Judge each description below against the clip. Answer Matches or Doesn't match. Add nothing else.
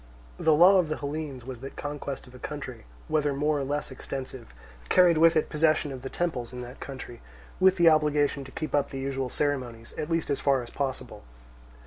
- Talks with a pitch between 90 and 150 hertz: Matches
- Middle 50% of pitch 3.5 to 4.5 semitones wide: Doesn't match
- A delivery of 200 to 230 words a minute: Matches